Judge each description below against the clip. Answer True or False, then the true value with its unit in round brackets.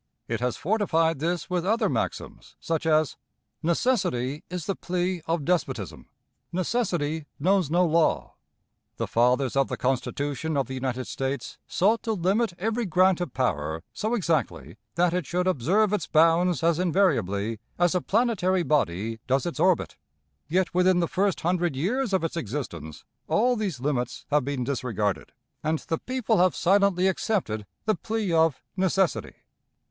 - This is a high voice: False (170 Hz)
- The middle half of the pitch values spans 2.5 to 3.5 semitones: False (5.6 semitones)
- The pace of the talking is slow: False (155 wpm)